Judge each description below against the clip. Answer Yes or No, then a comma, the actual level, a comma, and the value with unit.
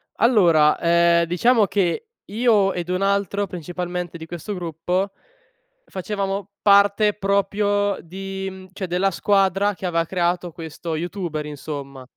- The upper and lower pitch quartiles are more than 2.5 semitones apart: Yes, average, 2.9 semitones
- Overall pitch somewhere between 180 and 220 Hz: Yes, medium, 185 Hz